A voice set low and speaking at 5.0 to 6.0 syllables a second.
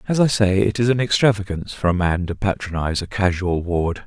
Yes: low, 100 Hz; 5.9 syllables/s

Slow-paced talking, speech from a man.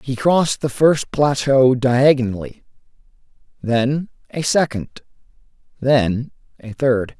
Yes: slow, 100 wpm; male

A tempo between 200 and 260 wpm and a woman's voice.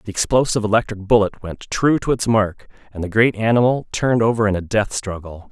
No: fast, 205 wpm; male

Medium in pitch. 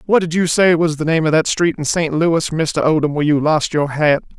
Yes: medium, 160 Hz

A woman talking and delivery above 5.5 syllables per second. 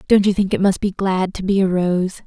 No: female; 5.3 syllables/s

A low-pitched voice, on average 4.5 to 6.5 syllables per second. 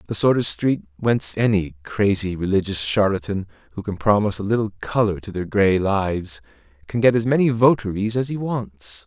Yes: low, 100 Hz; 5.3 syllables/s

